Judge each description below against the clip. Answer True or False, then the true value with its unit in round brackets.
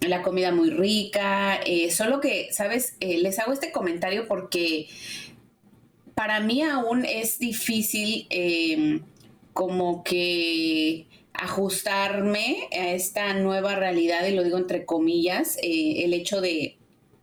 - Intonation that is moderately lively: True (3.8 semitones)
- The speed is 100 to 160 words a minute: True (125 wpm)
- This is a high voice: True (195 Hz)